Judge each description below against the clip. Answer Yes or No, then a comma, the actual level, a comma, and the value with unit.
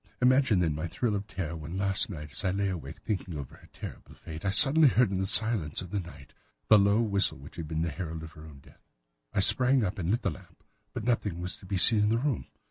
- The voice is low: Yes, very low, 95 Hz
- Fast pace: Yes, fast, 260 wpm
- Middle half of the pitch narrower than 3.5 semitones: No, average, 4.9 semitones